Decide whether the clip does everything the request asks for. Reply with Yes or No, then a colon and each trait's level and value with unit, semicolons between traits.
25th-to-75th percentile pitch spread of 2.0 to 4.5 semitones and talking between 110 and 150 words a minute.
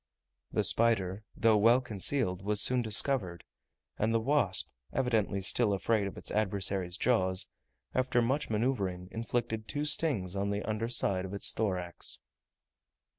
Yes: average, 3.8 semitones; average, 140 wpm